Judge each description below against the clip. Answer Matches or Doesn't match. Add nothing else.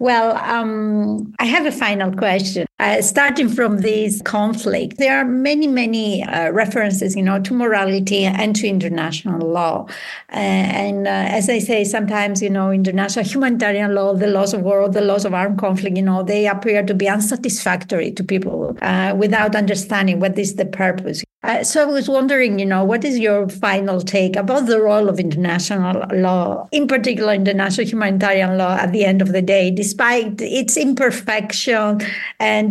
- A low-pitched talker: Doesn't match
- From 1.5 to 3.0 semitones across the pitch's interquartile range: Matches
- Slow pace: Doesn't match